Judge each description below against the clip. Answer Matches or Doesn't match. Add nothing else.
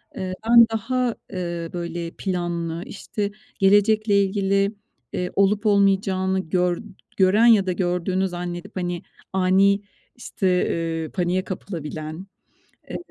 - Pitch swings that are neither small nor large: Doesn't match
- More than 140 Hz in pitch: Matches